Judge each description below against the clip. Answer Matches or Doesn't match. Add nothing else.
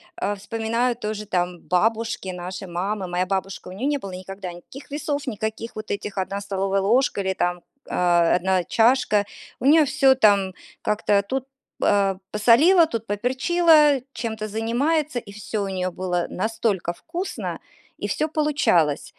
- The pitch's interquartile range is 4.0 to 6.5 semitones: Matches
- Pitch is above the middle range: Matches